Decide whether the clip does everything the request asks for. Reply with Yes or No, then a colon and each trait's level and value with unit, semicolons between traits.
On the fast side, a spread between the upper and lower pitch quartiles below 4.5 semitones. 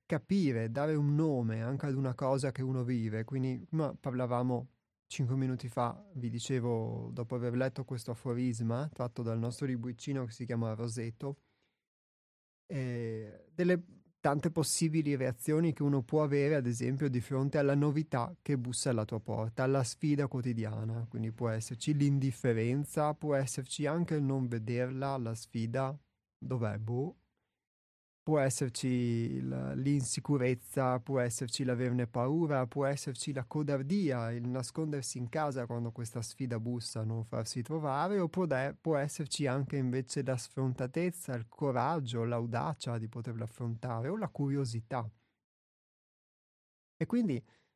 No: average, 140 wpm; average, 3.2 semitones